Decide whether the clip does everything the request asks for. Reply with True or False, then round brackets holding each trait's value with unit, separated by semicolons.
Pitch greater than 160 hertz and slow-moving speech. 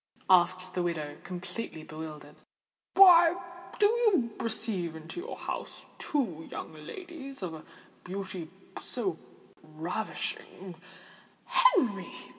True (185 Hz; 100 wpm)